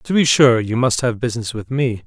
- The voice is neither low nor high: No, low, 125 Hz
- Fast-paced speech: Yes, fast, 260 wpm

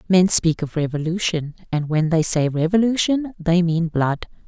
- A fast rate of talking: No, average, 160 wpm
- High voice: No, medium, 170 Hz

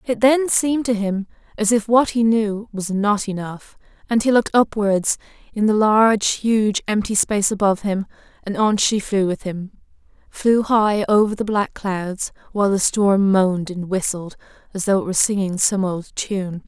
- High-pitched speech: Yes, high, 205 Hz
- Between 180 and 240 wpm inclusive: Yes, average, 185 wpm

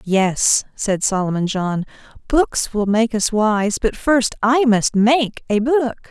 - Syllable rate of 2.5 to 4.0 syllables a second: Yes, 3.3 syllables/s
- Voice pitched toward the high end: Yes, high, 220 Hz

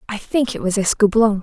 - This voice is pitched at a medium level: No, high, 210 Hz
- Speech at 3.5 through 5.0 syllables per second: No, 5.6 syllables/s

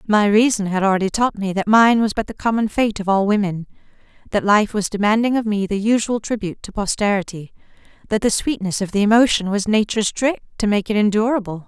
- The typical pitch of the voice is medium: No, high, 210 Hz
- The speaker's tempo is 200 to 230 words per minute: Yes, fast, 205 wpm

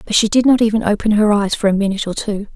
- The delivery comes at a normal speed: No, fast, 305 wpm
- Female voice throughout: Yes, female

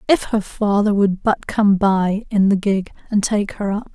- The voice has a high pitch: Yes, high, 205 Hz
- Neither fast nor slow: No, fast, 215 wpm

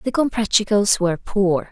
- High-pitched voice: Yes, high, 205 Hz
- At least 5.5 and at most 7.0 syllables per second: No, 5.0 syllables/s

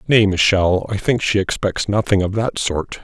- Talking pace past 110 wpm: Yes, average, 200 wpm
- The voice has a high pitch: No, low, 100 Hz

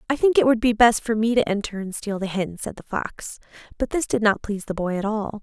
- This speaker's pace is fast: Yes, fast, 285 wpm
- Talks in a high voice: Yes, high, 220 Hz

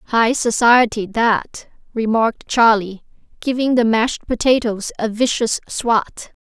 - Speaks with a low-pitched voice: No, high, 230 Hz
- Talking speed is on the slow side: Yes, slow, 110 wpm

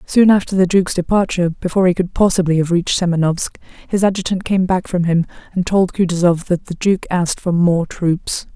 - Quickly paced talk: No, average, 180 wpm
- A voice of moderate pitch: Yes, medium, 180 Hz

